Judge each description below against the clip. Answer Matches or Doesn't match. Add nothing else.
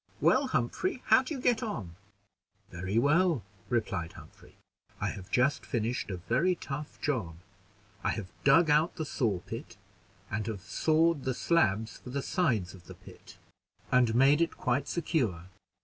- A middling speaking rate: Matches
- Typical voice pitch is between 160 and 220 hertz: Doesn't match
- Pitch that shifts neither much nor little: Doesn't match